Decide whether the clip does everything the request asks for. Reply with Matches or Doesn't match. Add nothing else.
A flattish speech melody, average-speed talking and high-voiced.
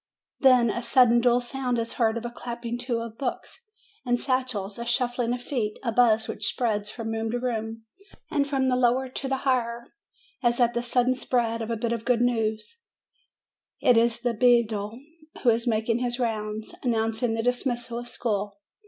Matches